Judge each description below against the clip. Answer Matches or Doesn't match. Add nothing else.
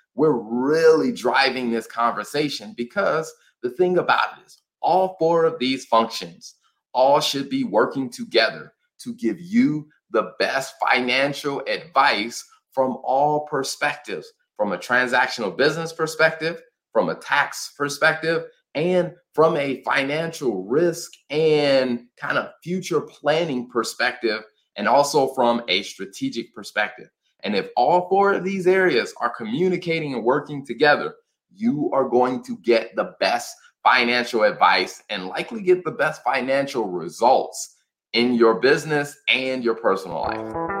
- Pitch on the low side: Doesn't match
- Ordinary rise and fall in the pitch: Doesn't match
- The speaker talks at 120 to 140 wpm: Matches